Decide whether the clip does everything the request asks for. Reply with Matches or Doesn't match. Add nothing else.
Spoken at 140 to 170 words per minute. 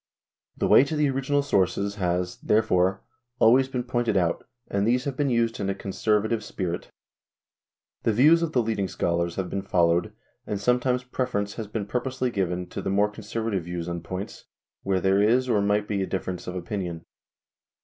Doesn't match